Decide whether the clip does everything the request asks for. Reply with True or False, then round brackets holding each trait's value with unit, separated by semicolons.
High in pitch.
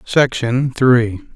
False (125 Hz)